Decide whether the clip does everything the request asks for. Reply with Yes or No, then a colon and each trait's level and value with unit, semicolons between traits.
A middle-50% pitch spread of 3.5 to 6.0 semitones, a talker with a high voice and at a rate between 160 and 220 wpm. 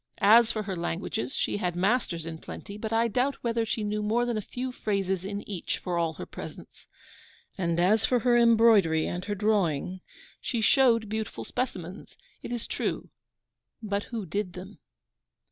Yes: average, 4.1 semitones; high, 210 Hz; average, 175 wpm